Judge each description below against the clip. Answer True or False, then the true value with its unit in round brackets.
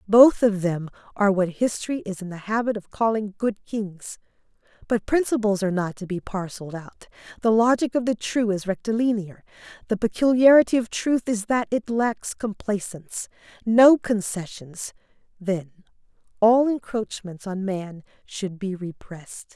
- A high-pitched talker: True (210 Hz)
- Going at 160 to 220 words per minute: False (145 wpm)